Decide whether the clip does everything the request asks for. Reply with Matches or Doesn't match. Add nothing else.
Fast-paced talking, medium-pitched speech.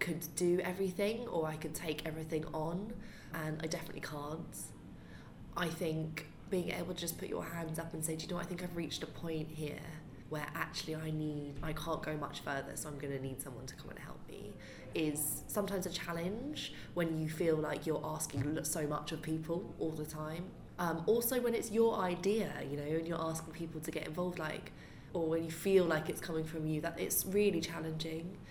Matches